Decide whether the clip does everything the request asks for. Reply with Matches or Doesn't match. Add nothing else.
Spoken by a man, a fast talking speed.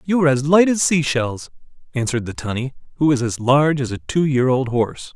Matches